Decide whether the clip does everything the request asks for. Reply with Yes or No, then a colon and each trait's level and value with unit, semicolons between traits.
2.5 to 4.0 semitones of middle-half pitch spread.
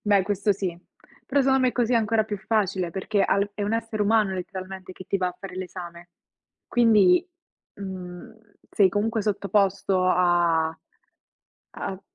Yes: average, 2.8 semitones